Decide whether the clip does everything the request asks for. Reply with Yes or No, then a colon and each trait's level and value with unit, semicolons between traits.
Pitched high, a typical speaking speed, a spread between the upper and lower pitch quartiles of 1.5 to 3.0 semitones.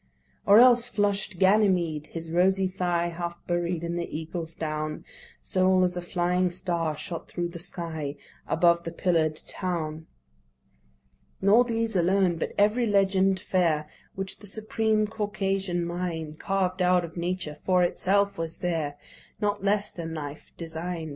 No: medium, 180 Hz; average, 145 wpm; average, 2.7 semitones